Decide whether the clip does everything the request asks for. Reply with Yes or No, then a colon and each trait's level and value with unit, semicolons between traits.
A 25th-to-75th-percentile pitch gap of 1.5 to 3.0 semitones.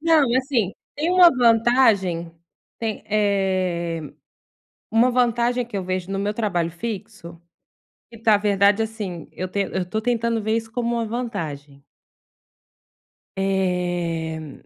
No: average, 4.5 semitones